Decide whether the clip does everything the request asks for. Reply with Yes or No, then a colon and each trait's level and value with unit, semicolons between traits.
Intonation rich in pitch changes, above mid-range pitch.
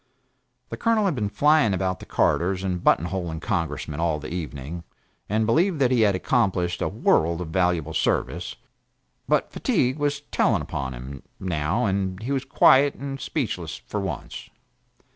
No: wide, 7.6 semitones; very low, 95 Hz